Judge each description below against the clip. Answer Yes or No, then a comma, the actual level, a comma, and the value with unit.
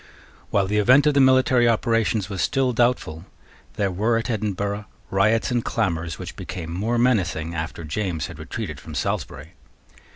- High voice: No, low, 105 Hz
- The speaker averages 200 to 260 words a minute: No, average, 160 wpm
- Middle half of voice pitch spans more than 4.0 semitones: Yes, average, 5.2 semitones